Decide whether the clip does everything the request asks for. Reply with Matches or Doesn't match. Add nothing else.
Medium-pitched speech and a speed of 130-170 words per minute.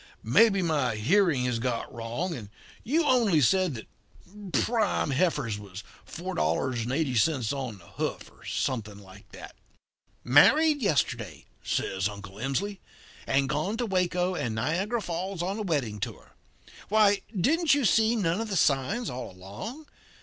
Matches